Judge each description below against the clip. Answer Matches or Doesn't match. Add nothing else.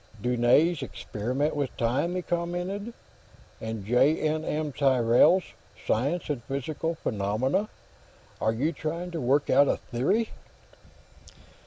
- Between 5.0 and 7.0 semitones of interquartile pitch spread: Matches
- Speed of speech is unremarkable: Doesn't match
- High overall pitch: Doesn't match